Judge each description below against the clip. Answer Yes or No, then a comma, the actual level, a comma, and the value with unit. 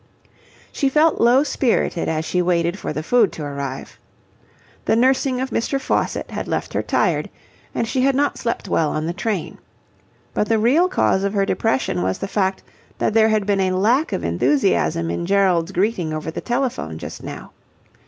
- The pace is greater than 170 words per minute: Yes, average, 185 wpm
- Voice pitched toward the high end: Yes, high, 200 Hz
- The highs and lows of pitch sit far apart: Yes, wide, 6.6 semitones